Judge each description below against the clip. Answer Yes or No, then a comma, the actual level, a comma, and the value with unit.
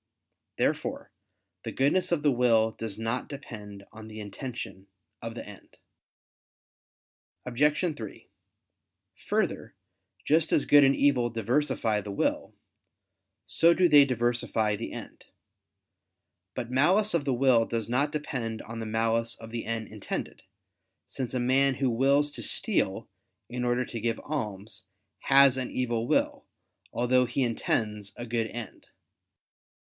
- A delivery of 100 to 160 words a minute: Yes, average, 140 wpm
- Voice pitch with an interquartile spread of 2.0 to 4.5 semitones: Yes, average, 3.5 semitones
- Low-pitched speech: Yes, low, 120 Hz